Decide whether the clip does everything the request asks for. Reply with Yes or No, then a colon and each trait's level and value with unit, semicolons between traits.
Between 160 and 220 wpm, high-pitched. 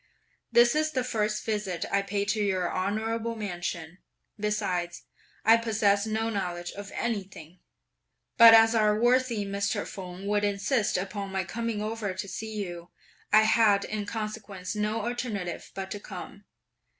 No: average, 150 wpm; high, 210 Hz